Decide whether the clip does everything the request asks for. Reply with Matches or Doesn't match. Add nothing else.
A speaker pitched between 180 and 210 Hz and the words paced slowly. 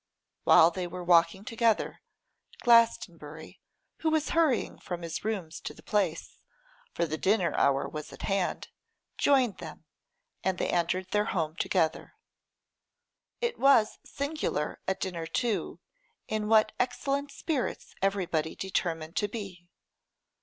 Matches